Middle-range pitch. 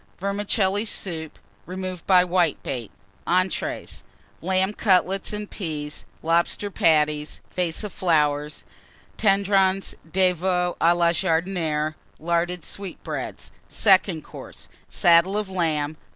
Yes: medium, 180 Hz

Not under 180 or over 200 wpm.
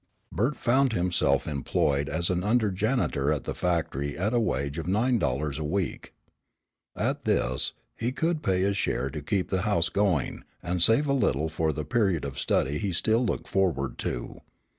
Yes: average, 185 wpm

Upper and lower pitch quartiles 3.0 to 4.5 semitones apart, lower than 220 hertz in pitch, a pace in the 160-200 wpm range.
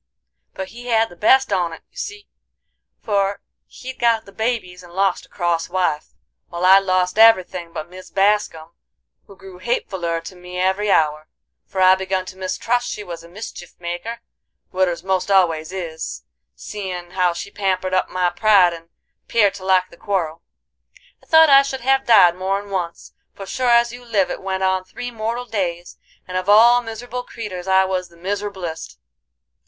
Yes: average, 3.3 semitones; high, 190 Hz; average, 175 wpm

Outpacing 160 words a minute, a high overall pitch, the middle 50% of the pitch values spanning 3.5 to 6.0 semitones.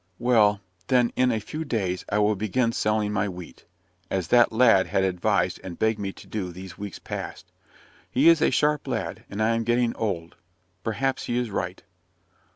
No: average, 185 wpm; low, 110 Hz; average, 4.0 semitones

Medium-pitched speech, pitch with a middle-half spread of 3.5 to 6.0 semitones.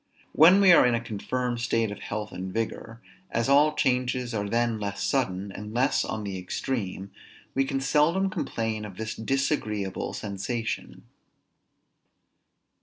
No: low, 115 Hz; average, 4.4 semitones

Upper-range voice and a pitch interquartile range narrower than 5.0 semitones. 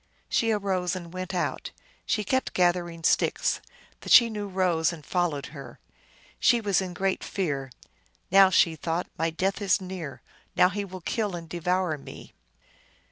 No: medium, 180 Hz; average, 2.7 semitones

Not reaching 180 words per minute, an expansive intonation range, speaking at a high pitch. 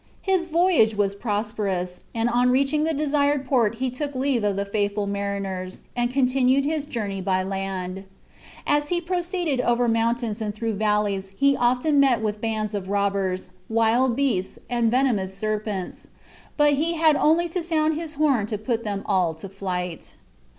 Yes: average, 165 wpm; wide, 5.7 semitones; high, 230 Hz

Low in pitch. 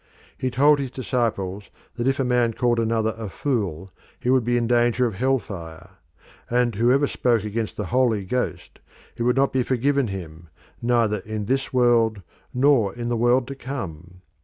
Yes: low, 120 Hz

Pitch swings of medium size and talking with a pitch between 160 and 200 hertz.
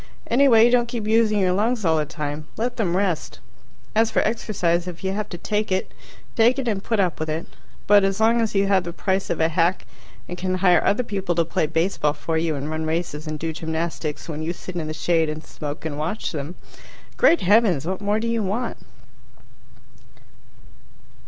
Yes: average, 5.0 semitones; medium, 185 Hz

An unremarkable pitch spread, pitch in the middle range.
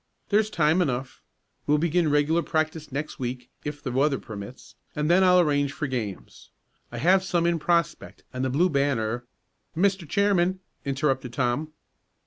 Yes: average, 4.7 semitones; medium, 150 Hz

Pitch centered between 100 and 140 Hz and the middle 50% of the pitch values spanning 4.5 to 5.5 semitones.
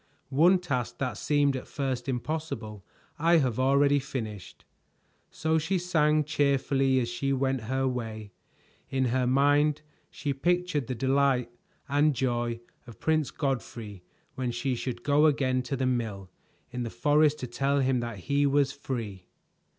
No: low, 135 Hz; average, 3.0 semitones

